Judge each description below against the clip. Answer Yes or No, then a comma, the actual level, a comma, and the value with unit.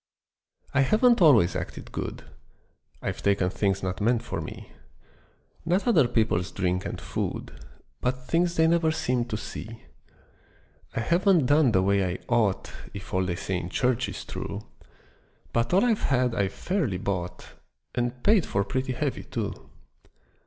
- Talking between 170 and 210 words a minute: No, average, 155 wpm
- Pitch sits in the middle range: No, low, 120 Hz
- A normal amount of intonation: No, wide, 8.2 semitones